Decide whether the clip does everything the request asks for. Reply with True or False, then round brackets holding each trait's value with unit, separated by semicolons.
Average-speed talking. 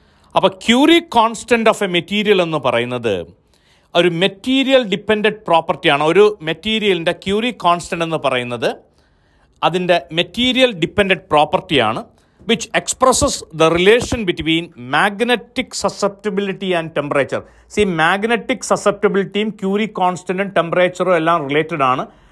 True (110 wpm)